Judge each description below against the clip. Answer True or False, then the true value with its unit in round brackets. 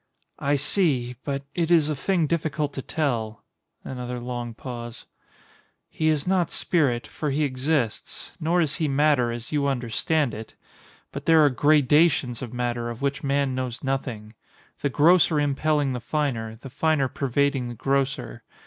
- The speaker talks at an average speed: True (160 wpm)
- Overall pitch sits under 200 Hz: True (140 Hz)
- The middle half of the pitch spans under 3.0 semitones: False (3.7 semitones)